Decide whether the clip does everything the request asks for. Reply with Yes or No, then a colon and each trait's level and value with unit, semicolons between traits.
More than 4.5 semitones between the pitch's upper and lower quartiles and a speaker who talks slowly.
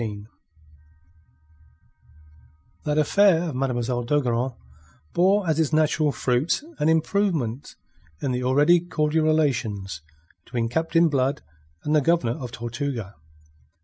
Yes: average, 4.9 semitones; slow, 115 wpm